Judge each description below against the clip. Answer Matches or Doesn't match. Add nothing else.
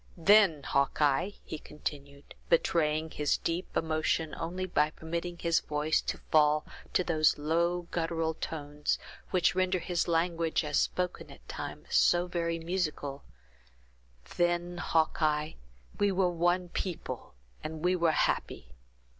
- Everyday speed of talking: Doesn't match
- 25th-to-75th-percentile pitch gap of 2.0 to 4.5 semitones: Matches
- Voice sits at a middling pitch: Matches